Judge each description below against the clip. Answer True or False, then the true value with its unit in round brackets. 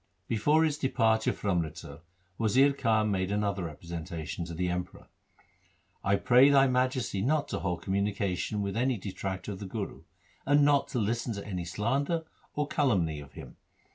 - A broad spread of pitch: True (5.9 semitones)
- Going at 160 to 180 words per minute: True (170 wpm)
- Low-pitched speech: True (105 Hz)